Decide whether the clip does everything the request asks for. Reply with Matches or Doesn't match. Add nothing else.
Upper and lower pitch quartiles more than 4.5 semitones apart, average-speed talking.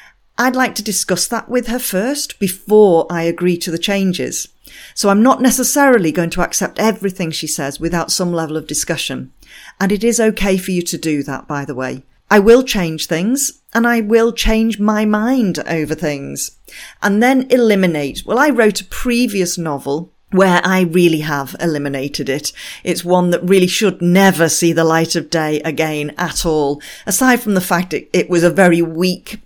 Matches